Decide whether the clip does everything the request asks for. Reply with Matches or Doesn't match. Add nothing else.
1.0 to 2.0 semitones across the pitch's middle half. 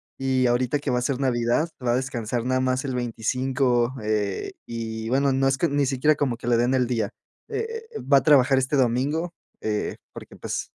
Doesn't match